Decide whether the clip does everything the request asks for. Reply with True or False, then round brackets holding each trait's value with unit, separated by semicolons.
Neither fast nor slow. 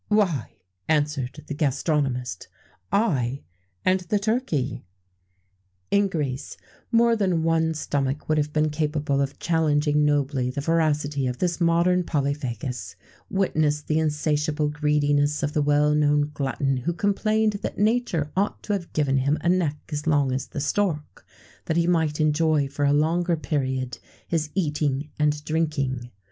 True (145 wpm)